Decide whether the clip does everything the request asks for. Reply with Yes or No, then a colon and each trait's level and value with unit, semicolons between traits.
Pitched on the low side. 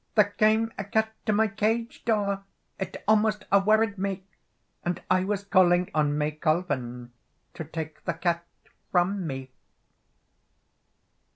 No: high, 190 Hz